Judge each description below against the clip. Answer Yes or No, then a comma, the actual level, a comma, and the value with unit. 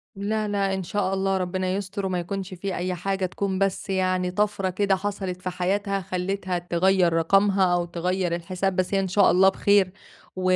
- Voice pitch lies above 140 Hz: Yes, high, 190 Hz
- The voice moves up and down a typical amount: No, narrow, 1.4 semitones